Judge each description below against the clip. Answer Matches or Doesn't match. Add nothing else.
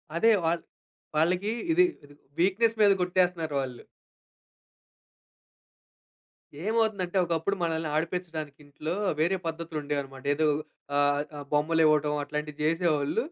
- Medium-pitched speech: Matches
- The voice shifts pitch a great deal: Doesn't match